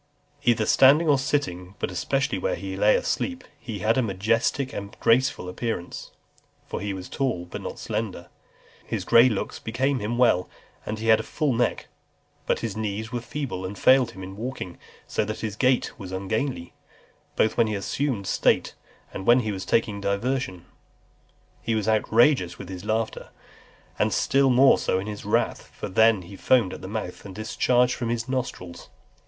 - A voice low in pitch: Yes, low, 110 Hz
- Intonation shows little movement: No, average, 4.5 semitones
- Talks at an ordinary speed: Yes, average, 180 wpm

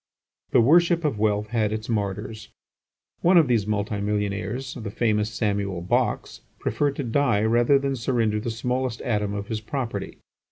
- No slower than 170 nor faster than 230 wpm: No, average, 160 wpm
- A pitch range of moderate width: Yes, average, 3.4 semitones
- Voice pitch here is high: No, low, 110 Hz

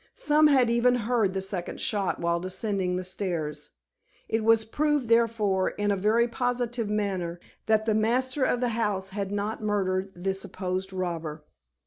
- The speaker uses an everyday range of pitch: Yes, average, 3.8 semitones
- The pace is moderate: Yes, average, 160 wpm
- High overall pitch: Yes, high, 210 Hz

